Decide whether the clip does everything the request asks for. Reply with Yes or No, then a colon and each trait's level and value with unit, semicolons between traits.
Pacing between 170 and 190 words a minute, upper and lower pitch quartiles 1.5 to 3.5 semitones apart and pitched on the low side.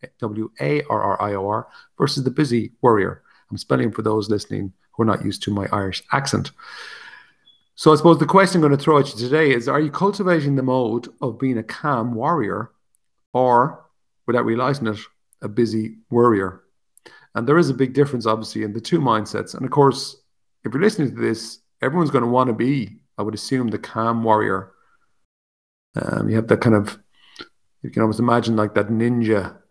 No: average, 185 wpm; average, 3.9 semitones; low, 120 Hz